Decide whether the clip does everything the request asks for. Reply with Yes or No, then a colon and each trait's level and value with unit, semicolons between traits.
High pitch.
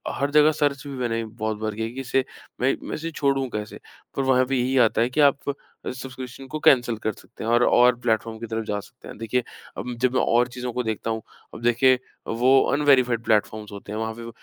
No: low, 125 Hz